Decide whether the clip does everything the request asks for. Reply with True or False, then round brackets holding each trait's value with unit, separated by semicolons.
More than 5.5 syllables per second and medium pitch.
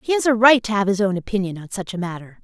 False (7.0 syllables/s; 205 Hz)